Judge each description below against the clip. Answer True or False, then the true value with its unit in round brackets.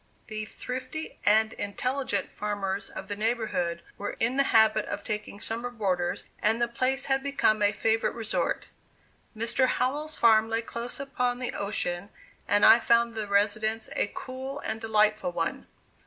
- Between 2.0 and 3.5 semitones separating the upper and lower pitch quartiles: True (3.2 semitones)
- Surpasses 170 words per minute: False (155 wpm)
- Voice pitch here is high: True (220 Hz)